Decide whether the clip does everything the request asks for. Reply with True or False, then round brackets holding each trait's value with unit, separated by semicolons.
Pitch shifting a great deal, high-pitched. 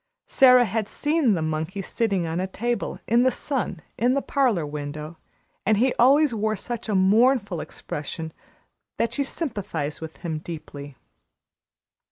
True (7.3 semitones; 205 Hz)